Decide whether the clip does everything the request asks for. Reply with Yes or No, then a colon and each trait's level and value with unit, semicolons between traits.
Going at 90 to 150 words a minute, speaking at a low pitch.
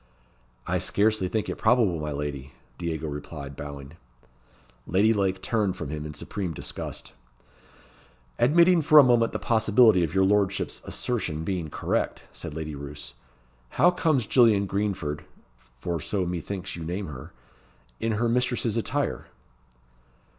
Yes: average, 140 wpm; very low, 95 Hz